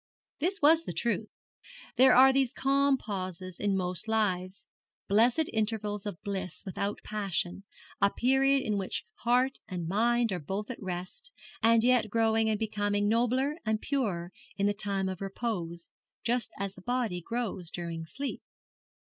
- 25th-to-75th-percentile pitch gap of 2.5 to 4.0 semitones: No, average, 4.4 semitones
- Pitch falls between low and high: No, high, 215 Hz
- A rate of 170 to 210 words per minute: No, average, 155 wpm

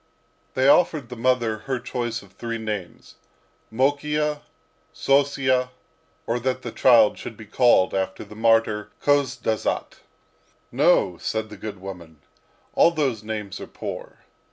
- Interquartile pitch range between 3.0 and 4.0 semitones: Yes, average, 3.6 semitones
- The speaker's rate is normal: No, slow, 130 wpm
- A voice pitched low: Yes, low, 115 Hz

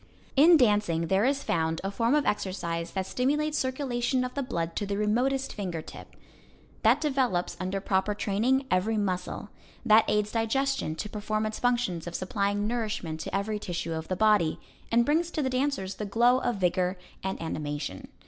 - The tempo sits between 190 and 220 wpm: No, average, 175 wpm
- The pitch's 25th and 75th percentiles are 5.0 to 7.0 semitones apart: Yes, wide, 5.4 semitones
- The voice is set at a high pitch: Yes, high, 210 Hz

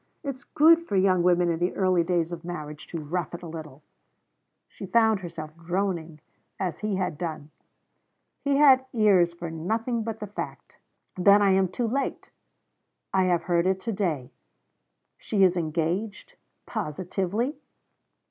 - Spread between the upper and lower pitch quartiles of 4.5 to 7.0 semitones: No, average, 4.0 semitones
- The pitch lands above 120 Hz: Yes, medium, 185 Hz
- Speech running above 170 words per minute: No, average, 155 wpm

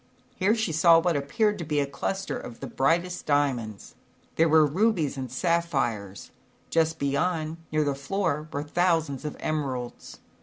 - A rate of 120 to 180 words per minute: Yes, average, 155 wpm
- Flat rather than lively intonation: No, average, 3.5 semitones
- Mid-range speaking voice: Yes, medium, 155 Hz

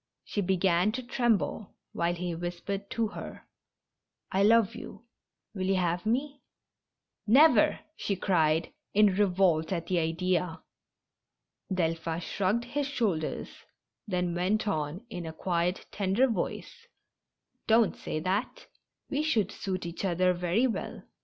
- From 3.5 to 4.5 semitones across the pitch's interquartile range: Yes, average, 4.0 semitones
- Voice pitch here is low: No, high, 190 Hz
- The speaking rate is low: Yes, slow, 120 wpm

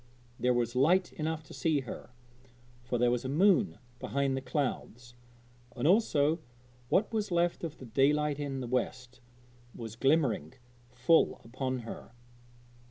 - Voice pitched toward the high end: No, low, 135 Hz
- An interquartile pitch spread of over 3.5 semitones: Yes, average, 4.5 semitones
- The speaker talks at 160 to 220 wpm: No, average, 145 wpm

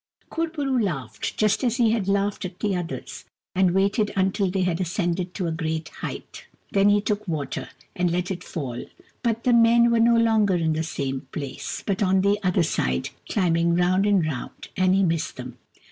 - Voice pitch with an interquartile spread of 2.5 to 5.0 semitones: Yes, average, 3.8 semitones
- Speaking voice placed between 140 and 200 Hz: Yes, medium, 185 Hz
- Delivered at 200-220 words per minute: Yes, fast, 205 wpm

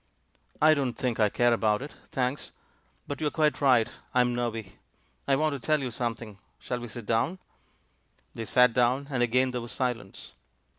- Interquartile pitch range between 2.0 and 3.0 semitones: Yes, average, 2.7 semitones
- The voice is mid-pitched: No, low, 125 Hz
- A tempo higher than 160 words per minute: Yes, average, 185 wpm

